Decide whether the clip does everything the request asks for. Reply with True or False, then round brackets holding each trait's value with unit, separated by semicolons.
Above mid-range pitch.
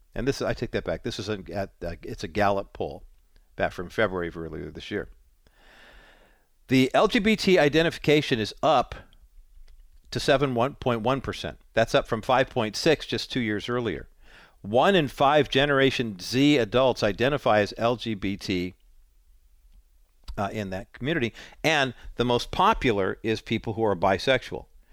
False (115 Hz)